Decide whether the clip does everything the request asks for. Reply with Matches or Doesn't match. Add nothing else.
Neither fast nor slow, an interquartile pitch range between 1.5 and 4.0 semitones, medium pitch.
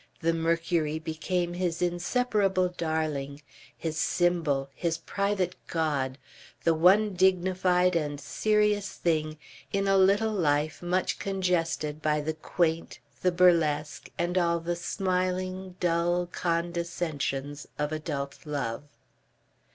Doesn't match